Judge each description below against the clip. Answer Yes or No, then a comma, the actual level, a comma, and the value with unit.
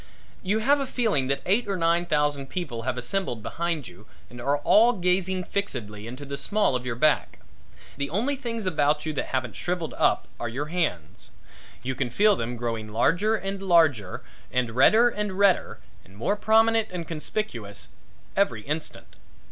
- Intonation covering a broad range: Yes, wide, 8.0 semitones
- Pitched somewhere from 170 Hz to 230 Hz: No, medium, 160 Hz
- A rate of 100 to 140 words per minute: No, average, 170 wpm